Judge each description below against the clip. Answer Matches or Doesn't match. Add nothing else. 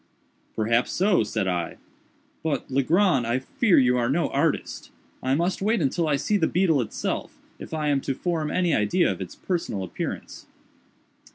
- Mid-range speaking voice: Matches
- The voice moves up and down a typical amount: Doesn't match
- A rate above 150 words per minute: Matches